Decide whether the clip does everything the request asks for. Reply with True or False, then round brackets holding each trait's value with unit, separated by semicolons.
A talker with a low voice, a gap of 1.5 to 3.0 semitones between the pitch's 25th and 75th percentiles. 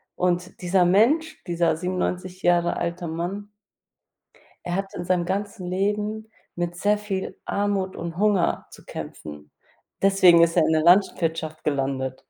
False (180 Hz; 2.7 semitones)